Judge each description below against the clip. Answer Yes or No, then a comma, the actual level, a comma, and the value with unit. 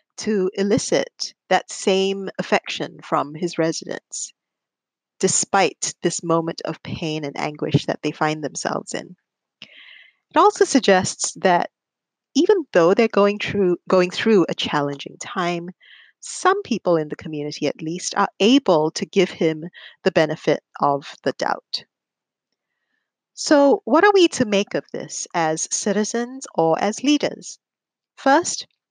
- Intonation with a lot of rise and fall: Yes, wide, 6.0 semitones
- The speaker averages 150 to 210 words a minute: No, slow, 135 wpm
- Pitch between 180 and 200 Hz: Yes, high, 190 Hz